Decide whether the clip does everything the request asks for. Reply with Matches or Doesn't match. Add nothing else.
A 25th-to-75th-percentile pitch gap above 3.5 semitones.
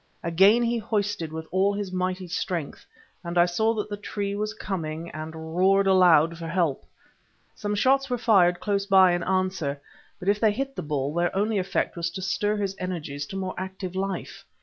Doesn't match